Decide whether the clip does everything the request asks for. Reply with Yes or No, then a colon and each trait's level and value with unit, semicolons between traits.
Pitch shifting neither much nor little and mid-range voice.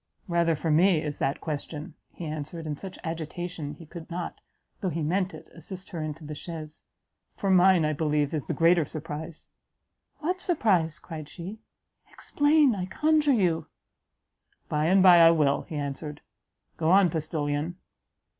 Yes: average, 3.1 semitones; medium, 165 Hz